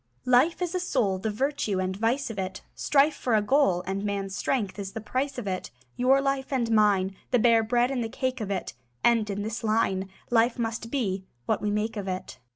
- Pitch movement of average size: Yes, average, 4.5 semitones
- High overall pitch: Yes, high, 225 Hz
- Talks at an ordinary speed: No, fast, 220 wpm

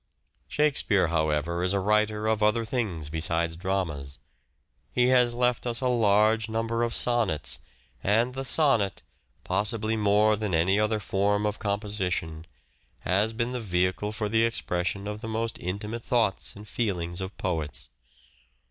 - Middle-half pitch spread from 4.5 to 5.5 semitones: No, average, 3.8 semitones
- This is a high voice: No, low, 105 Hz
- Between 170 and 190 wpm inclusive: No, average, 150 wpm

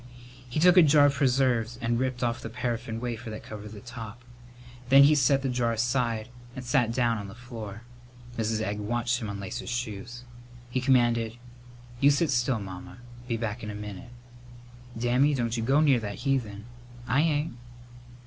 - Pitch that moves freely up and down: No, average, 2.7 semitones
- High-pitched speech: No, low, 120 Hz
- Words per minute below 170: No, average, 180 wpm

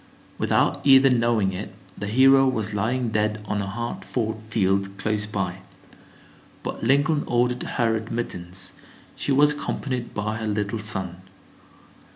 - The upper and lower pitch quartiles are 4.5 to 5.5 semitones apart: No, average, 3.3 semitones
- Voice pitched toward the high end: No, low, 110 Hz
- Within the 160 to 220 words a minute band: No, average, 140 wpm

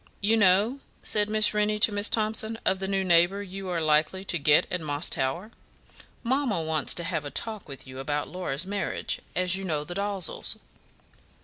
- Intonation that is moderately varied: Yes, average, 4.7 semitones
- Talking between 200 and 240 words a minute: No, average, 190 wpm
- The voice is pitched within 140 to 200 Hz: Yes, high, 190 Hz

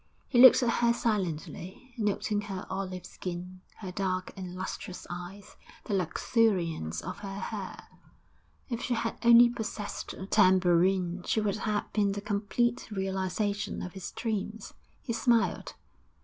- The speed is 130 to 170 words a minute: Yes, average, 140 wpm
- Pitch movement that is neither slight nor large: Yes, average, 3.2 semitones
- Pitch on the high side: Yes, high, 200 Hz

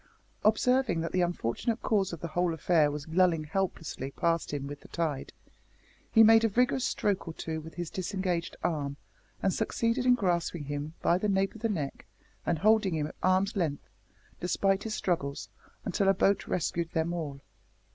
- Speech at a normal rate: Yes, average, 180 wpm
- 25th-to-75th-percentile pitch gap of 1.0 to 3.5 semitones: No, average, 4.0 semitones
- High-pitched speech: No, medium, 175 Hz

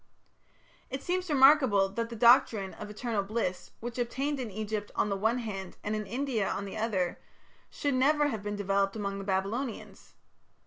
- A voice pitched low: No, high, 220 Hz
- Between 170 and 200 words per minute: Yes, average, 175 wpm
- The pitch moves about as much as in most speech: Yes, average, 4.3 semitones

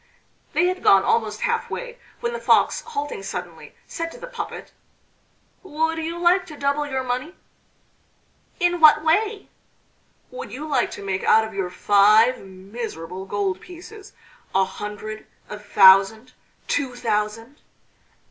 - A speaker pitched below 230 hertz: No, very high, 255 Hz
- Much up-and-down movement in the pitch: Yes, wide, 8.5 semitones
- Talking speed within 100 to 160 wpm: Yes, average, 140 wpm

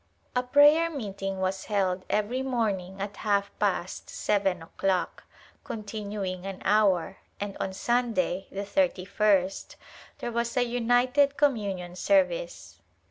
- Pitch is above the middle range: Yes, high, 205 Hz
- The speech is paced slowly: Yes, slow, 125 wpm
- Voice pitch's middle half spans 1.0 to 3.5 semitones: No, average, 4.3 semitones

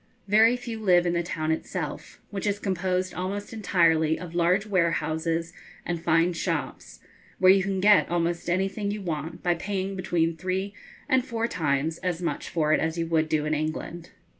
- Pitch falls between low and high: Yes, medium, 175 Hz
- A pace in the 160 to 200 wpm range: Yes, average, 180 wpm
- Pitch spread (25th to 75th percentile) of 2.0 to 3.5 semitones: Yes, average, 3.0 semitones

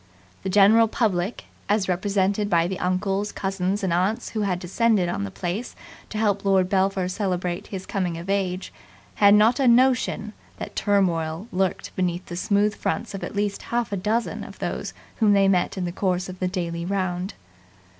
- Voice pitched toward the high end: Yes, high, 195 Hz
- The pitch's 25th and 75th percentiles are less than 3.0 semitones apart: Yes, narrow, 2.4 semitones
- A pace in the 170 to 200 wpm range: Yes, average, 185 wpm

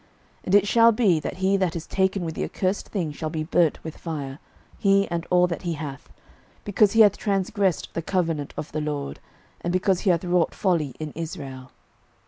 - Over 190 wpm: Yes, fast, 205 wpm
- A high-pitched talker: No, medium, 175 Hz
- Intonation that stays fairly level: No, average, 3.7 semitones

